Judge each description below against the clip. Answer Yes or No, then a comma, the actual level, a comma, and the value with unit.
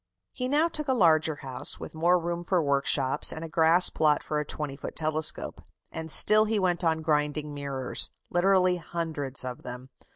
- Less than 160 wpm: No, average, 185 wpm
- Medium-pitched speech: Yes, medium, 160 Hz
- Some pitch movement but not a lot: Yes, average, 3.2 semitones